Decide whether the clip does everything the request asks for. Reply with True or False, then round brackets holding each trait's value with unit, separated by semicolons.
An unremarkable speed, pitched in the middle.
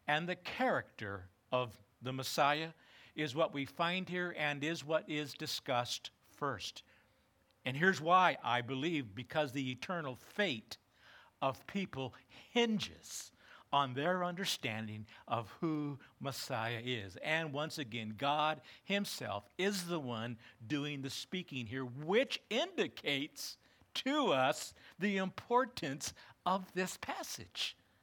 False (120 wpm; 150 Hz)